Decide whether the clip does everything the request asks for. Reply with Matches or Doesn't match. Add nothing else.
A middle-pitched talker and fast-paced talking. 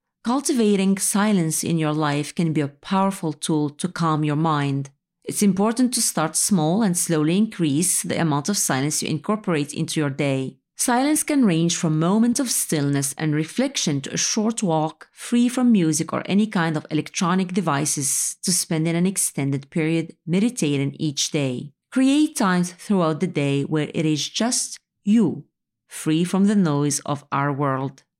Doesn't match